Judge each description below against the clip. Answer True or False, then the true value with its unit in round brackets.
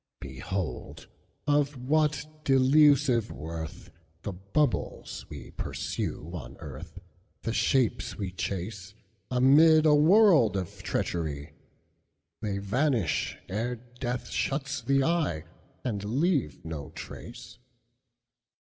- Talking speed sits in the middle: False (85 wpm)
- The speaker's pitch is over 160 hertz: False (115 Hz)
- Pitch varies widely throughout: True (8.5 semitones)